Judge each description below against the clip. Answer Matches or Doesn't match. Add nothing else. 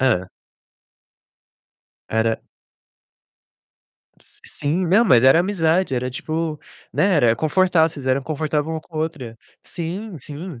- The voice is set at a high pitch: Doesn't match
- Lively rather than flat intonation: Doesn't match